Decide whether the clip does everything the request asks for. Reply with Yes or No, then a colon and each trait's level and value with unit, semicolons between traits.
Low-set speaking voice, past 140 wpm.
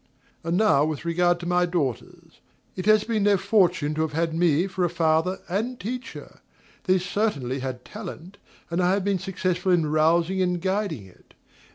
No: medium, 180 Hz; average, 180 wpm